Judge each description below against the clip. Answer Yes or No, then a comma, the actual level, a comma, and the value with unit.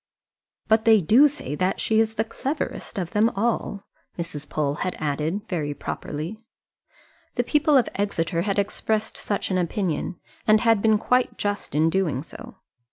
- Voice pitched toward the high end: Yes, high, 200 Hz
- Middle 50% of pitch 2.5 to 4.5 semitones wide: No, average, 4.9 semitones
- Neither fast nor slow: Yes, average, 165 wpm